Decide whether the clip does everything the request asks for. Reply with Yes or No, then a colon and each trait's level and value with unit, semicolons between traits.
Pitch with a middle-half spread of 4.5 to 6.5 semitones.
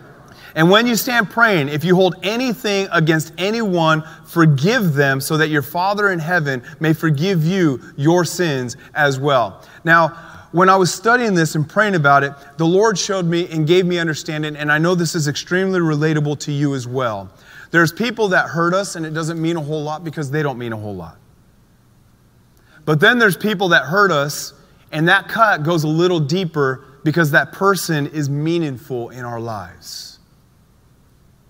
No: average, 4.0 semitones